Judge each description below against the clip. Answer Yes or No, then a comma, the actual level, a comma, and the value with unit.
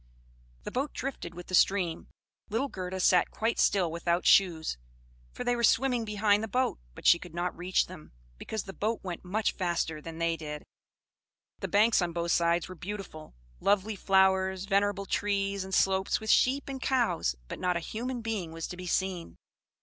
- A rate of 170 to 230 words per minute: Yes, average, 185 wpm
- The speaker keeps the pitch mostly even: No, average, 3.8 semitones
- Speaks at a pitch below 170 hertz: No, high, 190 Hz